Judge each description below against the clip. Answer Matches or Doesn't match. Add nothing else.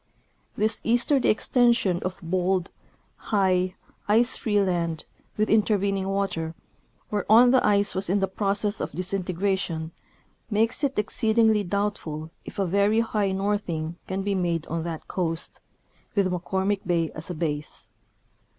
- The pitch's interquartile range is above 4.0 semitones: Doesn't match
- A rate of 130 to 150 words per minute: Matches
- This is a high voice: Matches